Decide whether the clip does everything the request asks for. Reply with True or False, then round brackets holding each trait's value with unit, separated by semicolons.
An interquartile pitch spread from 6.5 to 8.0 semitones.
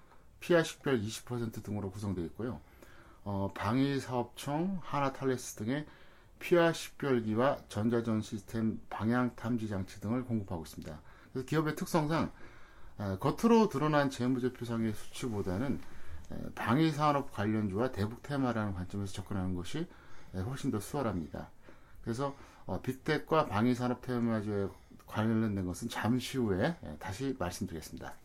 False (5.2 semitones)